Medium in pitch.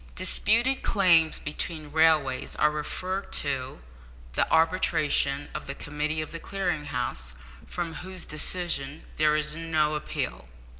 Yes: medium, 155 Hz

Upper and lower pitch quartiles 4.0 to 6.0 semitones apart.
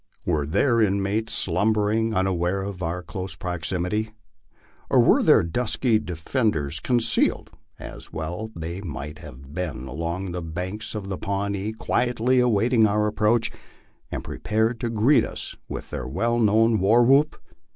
Yes: average, 4.3 semitones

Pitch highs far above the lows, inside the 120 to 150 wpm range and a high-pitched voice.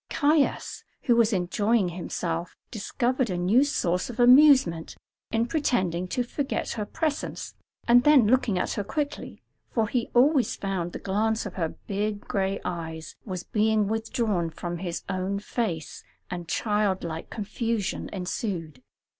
No: average, 5.0 semitones; average, 145 wpm; high, 210 Hz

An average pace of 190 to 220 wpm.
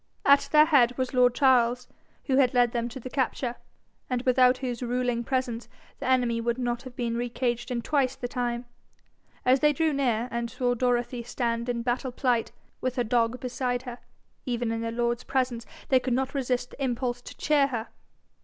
Yes: average, 195 wpm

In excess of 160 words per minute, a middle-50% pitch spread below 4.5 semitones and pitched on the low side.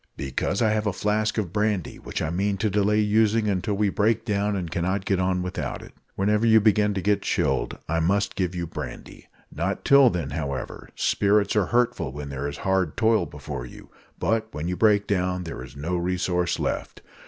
Yes: average, 200 wpm; average, 3.3 semitones; very low, 95 Hz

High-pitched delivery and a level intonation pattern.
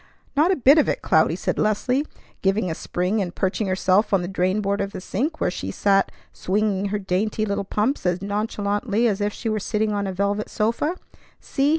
Yes: high, 205 Hz; narrow, 2.2 semitones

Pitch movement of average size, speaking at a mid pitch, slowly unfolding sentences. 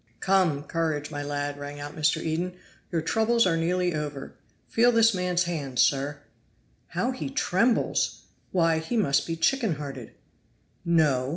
No: average, 4.2 semitones; medium, 165 Hz; average, 150 wpm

